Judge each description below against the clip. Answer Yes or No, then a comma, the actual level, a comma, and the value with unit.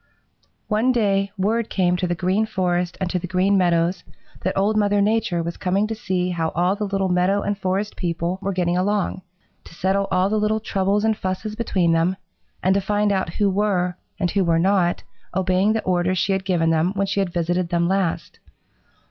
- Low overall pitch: No, high, 190 Hz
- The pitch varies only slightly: Yes, narrow, 2.3 semitones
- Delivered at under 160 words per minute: No, fast, 205 wpm